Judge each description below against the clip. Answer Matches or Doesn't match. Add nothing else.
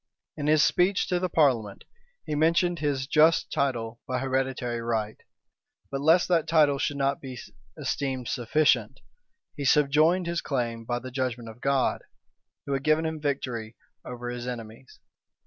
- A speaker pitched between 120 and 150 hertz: Matches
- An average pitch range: Matches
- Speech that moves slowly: Doesn't match